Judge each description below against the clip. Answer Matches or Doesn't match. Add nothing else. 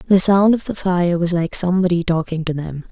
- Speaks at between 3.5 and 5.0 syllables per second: Doesn't match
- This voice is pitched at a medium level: Matches